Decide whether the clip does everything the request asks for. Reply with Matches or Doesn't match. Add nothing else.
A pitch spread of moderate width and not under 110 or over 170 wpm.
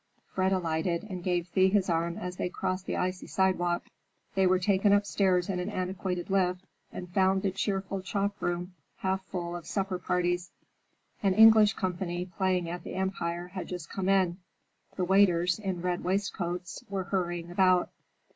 Doesn't match